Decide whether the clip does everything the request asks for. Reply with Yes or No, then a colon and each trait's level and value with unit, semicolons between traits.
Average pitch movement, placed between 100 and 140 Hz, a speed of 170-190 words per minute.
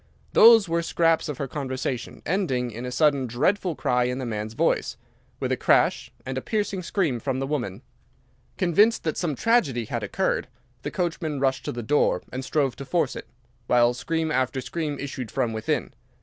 Yes: average, 5.0 semitones; low, 135 Hz; average, 185 wpm